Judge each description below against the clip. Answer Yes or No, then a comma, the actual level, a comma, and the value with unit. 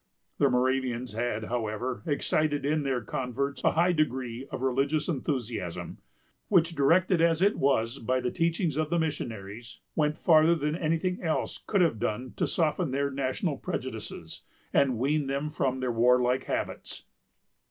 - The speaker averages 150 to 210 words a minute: Yes, average, 155 wpm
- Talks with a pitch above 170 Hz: No, medium, 140 Hz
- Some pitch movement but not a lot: Yes, average, 4.0 semitones